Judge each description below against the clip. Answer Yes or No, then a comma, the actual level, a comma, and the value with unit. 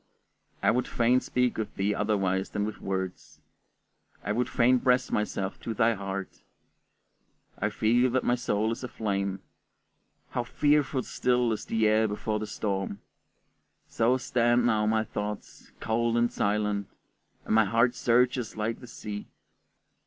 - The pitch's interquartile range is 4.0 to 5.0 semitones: No, average, 2.8 semitones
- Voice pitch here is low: Yes, low, 110 Hz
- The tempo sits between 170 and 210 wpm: No, average, 145 wpm